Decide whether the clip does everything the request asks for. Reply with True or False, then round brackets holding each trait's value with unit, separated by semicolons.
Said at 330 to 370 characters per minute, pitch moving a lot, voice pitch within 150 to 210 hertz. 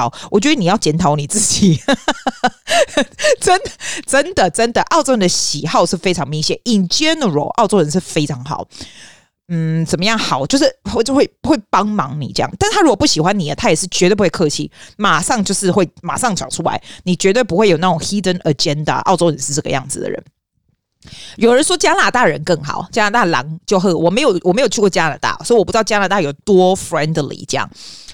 True (355 characters per minute; 6.5 semitones; 190 Hz)